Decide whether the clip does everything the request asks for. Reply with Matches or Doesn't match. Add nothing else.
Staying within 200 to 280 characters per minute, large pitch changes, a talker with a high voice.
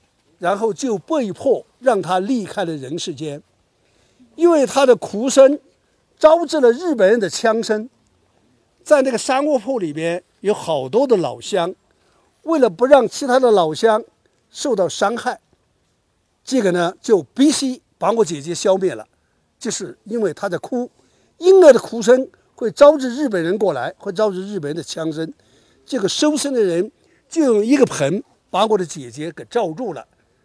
Matches